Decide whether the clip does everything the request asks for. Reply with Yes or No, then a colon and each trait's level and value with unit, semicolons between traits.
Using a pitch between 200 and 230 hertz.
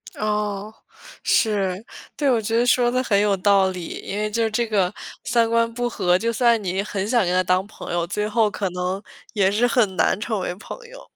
Yes: high, 210 Hz